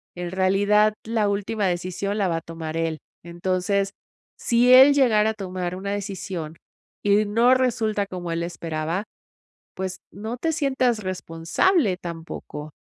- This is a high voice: Yes, high, 195 Hz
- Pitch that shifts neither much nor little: Yes, average, 3.9 semitones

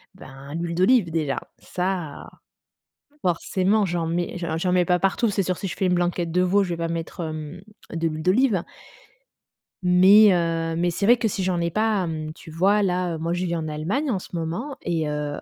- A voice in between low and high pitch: Yes, medium, 175 Hz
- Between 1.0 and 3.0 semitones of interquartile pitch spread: Yes, narrow, 2.6 semitones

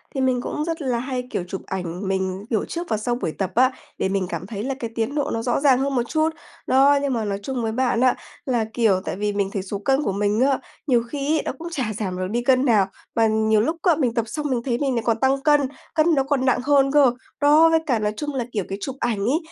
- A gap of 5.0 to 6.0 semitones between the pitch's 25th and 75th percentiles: No, average, 4.6 semitones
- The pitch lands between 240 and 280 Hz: Yes, high, 245 Hz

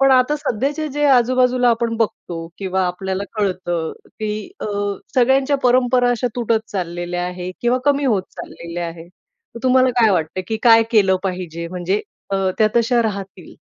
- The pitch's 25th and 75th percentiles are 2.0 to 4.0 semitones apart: No, wide, 5.4 semitones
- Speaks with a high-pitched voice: Yes, high, 215 Hz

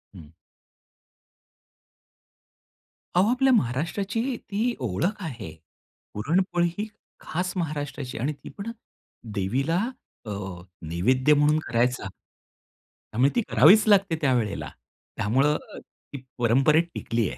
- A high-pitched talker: No, medium, 145 Hz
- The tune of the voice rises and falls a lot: Yes, wide, 7.0 semitones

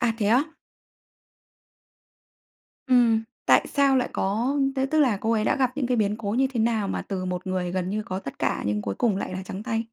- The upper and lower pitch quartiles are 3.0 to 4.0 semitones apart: No, average, 4.6 semitones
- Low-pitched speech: No, high, 220 Hz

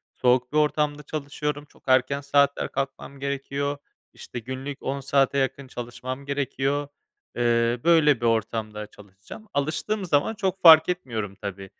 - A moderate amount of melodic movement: Yes, average, 3.3 semitones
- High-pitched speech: No, medium, 140 Hz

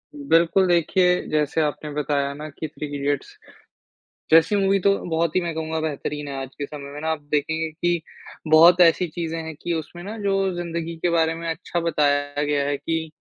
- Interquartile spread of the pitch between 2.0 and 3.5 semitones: Yes, narrow, 2.5 semitones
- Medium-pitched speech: Yes, medium, 160 Hz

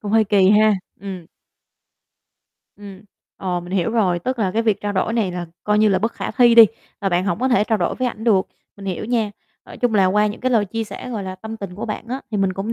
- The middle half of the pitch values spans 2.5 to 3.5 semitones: Yes, average, 3.0 semitones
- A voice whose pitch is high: Yes, high, 210 Hz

